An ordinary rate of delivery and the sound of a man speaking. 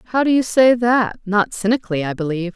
No: average, 190 wpm; female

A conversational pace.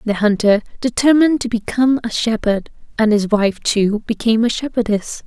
Yes: average, 160 wpm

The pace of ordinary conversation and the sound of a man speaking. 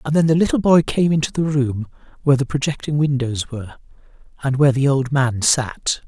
Yes: average, 195 wpm; male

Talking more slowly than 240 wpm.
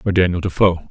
Yes: average, 200 wpm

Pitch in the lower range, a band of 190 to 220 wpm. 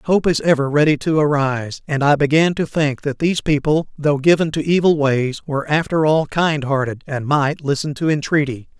No: medium, 150 Hz; average, 200 wpm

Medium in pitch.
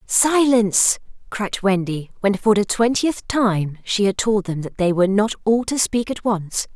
No: high, 210 Hz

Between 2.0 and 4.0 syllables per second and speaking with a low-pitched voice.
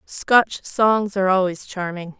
No: 3.9 syllables/s; high, 190 Hz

